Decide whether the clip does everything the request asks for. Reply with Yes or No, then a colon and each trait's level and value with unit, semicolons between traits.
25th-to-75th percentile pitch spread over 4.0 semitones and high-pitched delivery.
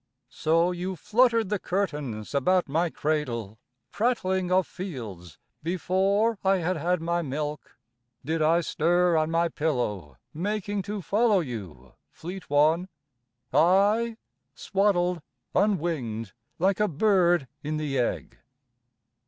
No: average, 4.4 semitones; medium, 175 Hz